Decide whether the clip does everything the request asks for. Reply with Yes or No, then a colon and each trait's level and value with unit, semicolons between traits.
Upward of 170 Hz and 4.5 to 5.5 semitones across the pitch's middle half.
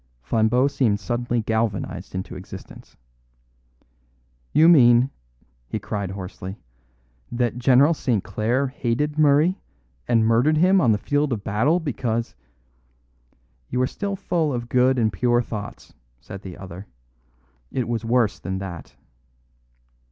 No: low, 120 Hz; average, 4.9 semitones